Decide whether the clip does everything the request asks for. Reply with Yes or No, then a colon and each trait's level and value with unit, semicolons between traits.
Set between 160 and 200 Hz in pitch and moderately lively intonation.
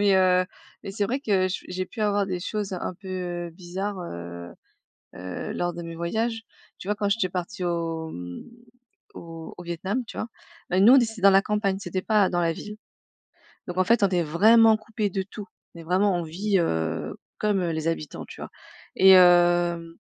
Yes: medium, 185 Hz; average, 3.3 semitones